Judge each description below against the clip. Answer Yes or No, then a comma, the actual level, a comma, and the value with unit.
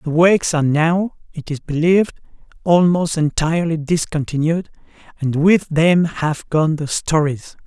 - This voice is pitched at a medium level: Yes, medium, 160 Hz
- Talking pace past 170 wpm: No, slow, 135 wpm